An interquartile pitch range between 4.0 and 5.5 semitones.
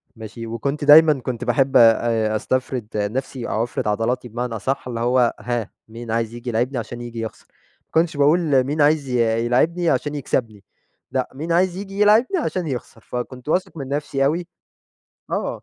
Yes: average, 4.3 semitones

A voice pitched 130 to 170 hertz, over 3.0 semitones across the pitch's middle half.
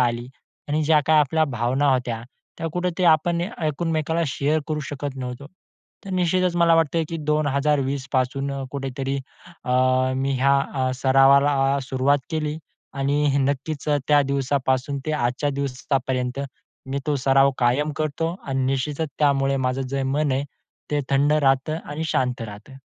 No: medium, 140 Hz; narrow, 2.4 semitones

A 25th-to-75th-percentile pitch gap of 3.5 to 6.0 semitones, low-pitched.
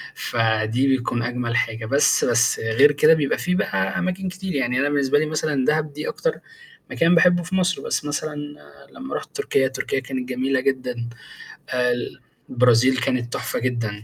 Yes: average, 4.3 semitones; low, 130 Hz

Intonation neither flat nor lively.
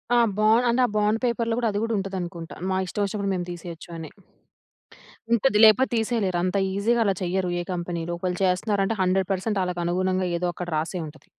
Yes: average, 3.3 semitones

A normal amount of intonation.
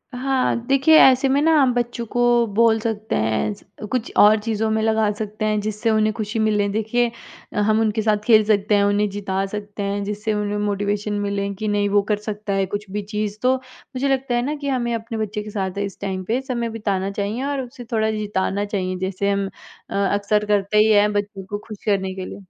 No: narrow, 2.1 semitones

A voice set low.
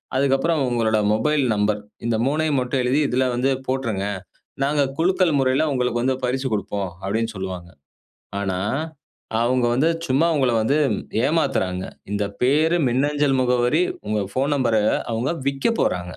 Yes: low, 130 Hz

